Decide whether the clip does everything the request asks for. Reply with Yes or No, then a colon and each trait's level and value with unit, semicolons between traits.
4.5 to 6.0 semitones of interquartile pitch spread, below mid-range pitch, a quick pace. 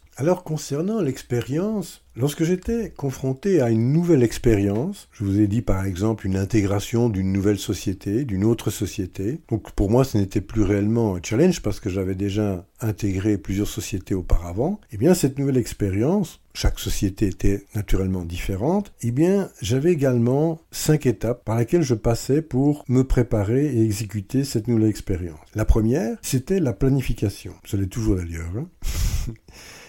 No: wide, 5.6 semitones; low, 115 Hz; average, 160 wpm